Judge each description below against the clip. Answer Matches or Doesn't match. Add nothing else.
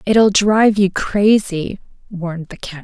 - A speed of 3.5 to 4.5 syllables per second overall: Matches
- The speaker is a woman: Matches